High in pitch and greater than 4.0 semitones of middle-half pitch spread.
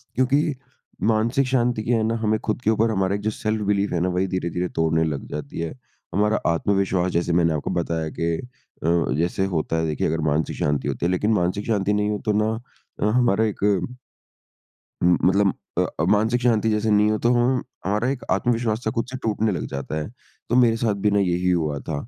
No: low, 105 Hz; average, 4.4 semitones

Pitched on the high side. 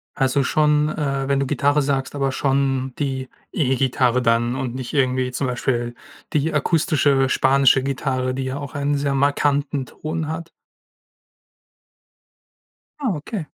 No: low, 135 Hz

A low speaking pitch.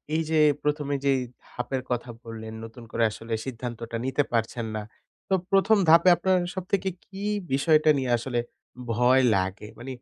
Yes: low, 130 Hz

